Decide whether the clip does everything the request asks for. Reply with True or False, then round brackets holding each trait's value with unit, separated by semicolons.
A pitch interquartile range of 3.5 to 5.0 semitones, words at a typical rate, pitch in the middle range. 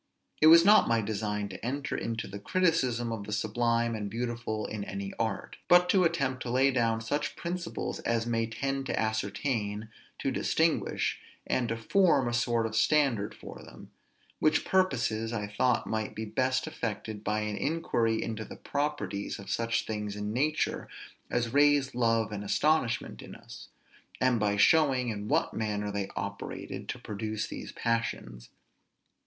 False (4.1 semitones; 165 wpm; 115 Hz)